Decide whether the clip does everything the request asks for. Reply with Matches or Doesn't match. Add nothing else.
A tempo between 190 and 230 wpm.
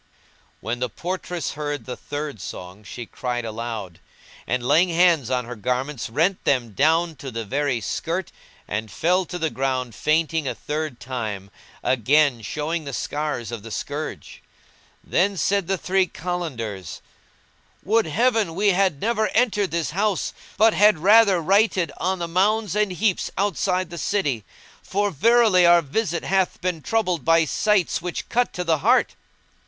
Doesn't match